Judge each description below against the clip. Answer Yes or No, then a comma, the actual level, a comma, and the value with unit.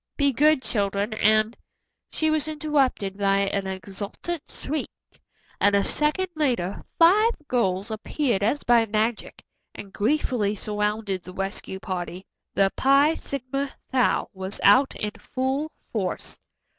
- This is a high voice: Yes, high, 220 Hz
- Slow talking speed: Yes, slow, 130 wpm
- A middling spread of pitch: No, wide, 6.0 semitones